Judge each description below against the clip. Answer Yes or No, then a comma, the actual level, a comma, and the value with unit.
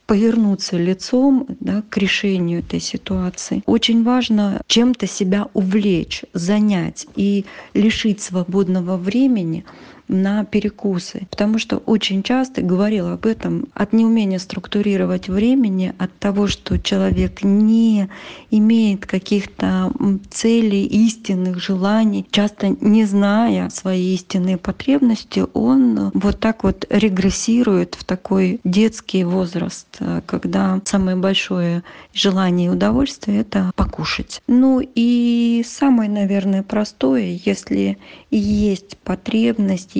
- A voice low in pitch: No, high, 205 Hz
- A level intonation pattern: No, average, 3.1 semitones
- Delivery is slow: Yes, slow, 105 wpm